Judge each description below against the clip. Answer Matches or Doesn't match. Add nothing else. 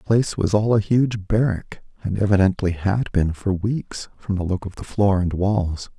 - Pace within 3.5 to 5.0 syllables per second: Matches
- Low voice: Matches